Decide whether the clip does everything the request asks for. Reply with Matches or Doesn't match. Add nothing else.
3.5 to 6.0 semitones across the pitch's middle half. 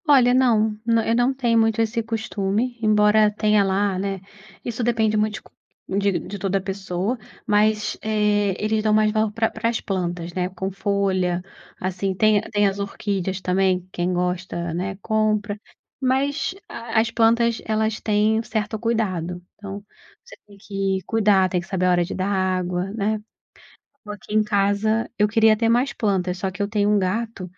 Doesn't match